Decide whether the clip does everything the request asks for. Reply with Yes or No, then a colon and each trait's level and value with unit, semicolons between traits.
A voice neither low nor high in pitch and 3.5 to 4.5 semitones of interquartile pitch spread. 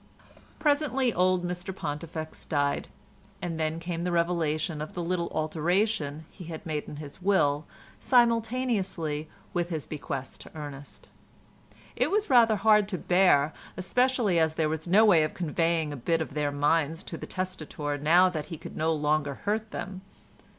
Yes: medium, 165 Hz; average, 3.8 semitones